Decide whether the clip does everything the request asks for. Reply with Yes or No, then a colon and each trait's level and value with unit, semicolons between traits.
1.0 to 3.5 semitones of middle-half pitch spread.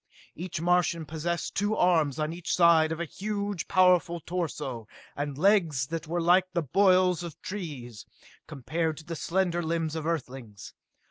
Yes: average, 2.7 semitones